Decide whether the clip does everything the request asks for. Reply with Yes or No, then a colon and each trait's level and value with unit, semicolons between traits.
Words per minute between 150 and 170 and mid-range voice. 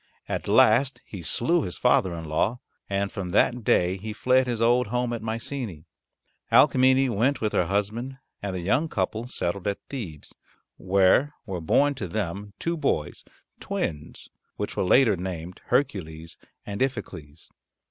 No: average, 155 wpm; low, 105 Hz